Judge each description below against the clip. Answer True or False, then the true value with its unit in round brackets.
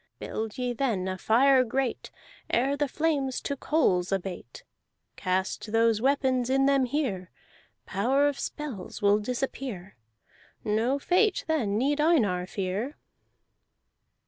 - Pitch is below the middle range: False (250 Hz)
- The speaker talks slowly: True (120 wpm)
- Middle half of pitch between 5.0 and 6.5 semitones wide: True (5.4 semitones)